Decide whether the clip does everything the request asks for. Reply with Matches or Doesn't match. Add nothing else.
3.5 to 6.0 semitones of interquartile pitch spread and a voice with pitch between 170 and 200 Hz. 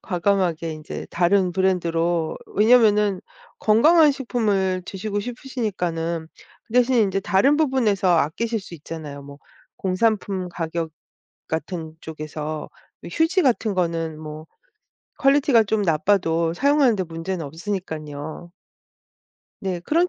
Matches